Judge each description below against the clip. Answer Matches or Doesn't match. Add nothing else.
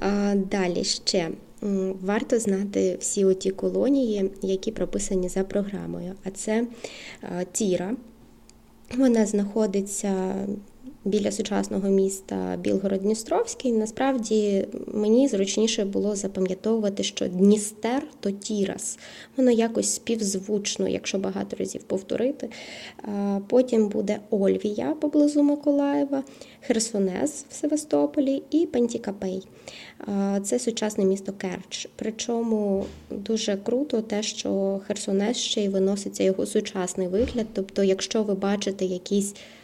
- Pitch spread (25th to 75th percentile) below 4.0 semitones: Matches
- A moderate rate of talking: Doesn't match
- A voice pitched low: Doesn't match